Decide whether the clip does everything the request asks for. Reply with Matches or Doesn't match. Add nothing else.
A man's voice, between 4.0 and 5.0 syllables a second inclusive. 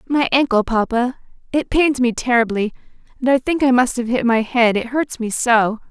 Doesn't match